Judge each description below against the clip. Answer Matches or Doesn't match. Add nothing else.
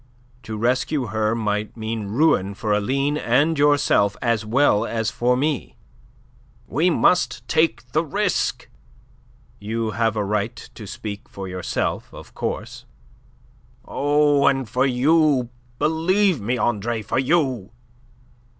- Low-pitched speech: Matches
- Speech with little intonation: Doesn't match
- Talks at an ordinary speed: Doesn't match